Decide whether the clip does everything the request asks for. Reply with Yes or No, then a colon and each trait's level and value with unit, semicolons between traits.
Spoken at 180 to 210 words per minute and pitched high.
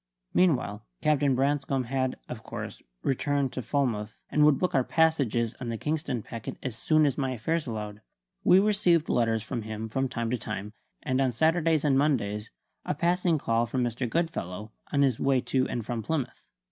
No: average, 185 wpm; low, 130 Hz